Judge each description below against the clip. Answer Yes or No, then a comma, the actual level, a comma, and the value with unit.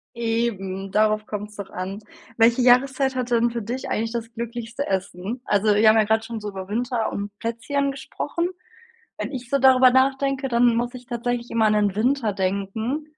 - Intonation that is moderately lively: Yes, average, 3.1 semitones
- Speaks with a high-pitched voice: Yes, high, 230 Hz